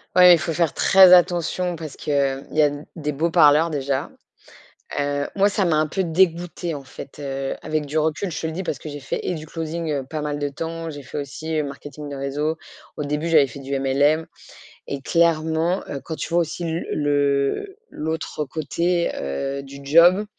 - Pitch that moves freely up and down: No, average, 2.8 semitones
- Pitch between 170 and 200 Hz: No, medium, 155 Hz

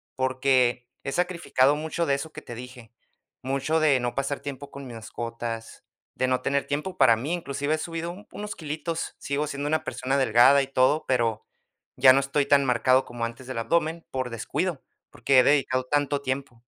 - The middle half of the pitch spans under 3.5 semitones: Yes, average, 2.9 semitones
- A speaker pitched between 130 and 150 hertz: Yes, low, 135 Hz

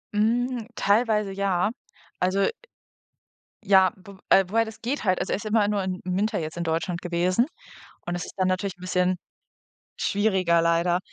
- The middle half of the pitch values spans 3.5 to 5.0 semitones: No, average, 2.8 semitones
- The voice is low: No, high, 190 Hz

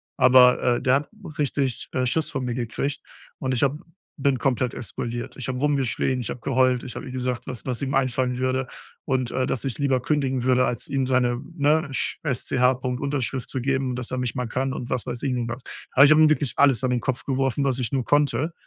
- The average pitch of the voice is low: Yes, low, 130 Hz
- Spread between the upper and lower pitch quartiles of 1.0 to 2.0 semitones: Yes, narrow, 1.6 semitones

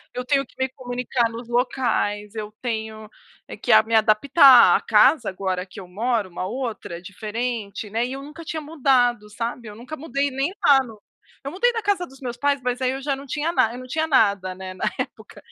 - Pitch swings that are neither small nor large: Yes, average, 4.3 semitones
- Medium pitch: No, high, 245 Hz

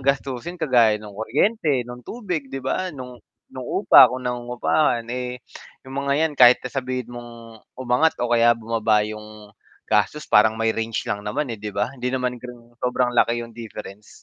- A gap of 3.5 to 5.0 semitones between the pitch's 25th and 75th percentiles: No, narrow, 2.6 semitones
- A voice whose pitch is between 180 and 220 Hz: No, low, 120 Hz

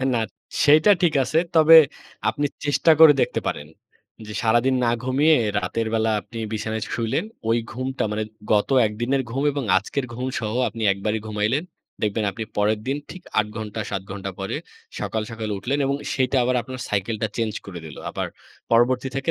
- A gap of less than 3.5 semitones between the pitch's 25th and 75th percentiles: No, average, 4.0 semitones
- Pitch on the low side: Yes, low, 115 Hz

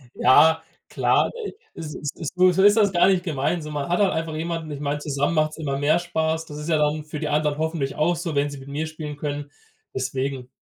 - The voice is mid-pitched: Yes, medium, 155 Hz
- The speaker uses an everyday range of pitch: No, narrow, 2.2 semitones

